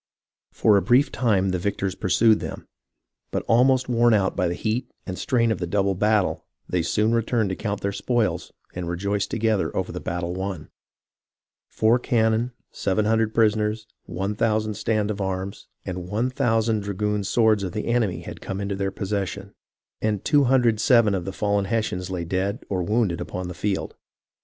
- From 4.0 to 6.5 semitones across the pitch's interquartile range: No, average, 2.9 semitones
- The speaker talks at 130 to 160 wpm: No, average, 170 wpm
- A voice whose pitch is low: Yes, low, 105 Hz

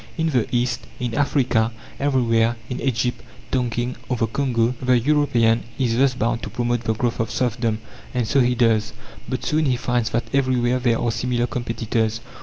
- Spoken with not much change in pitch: Yes, narrow, 1.9 semitones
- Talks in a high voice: No, low, 120 Hz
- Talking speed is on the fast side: No, average, 180 wpm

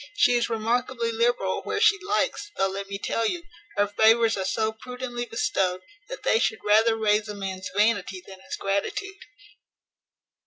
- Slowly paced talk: No, average, 165 wpm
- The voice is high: Yes, high, 220 Hz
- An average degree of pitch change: Yes, average, 3.3 semitones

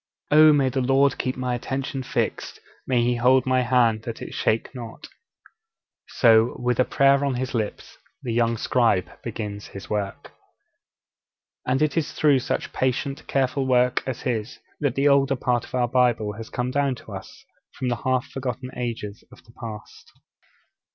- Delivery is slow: No, average, 170 wpm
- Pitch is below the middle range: Yes, low, 125 Hz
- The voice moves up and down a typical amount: No, narrow, 2.3 semitones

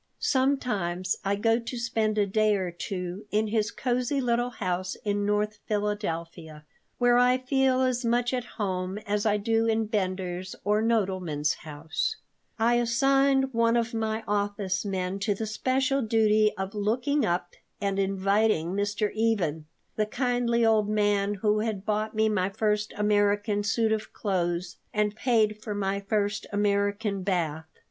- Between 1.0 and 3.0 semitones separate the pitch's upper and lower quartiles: Yes, narrow, 2.6 semitones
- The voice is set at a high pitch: Yes, high, 210 Hz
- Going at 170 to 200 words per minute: No, average, 155 wpm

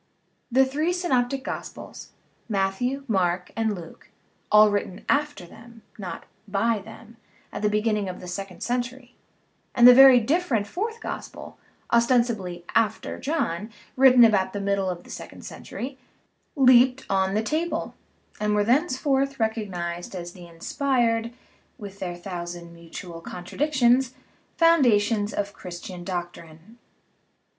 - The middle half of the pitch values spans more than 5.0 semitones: Yes, wide, 5.4 semitones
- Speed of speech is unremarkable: No, slow, 130 wpm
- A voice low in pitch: No, high, 220 Hz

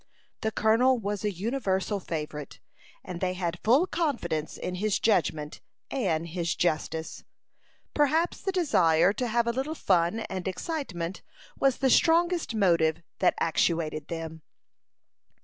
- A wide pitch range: Yes, wide, 7.1 semitones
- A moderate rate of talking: No, slow, 130 wpm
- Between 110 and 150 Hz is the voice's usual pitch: No, high, 190 Hz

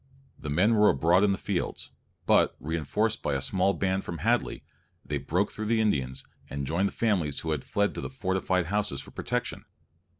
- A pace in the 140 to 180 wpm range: No, average, 195 wpm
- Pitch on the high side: No, very low, 95 Hz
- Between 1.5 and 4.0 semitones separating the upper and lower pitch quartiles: No, wide, 5.5 semitones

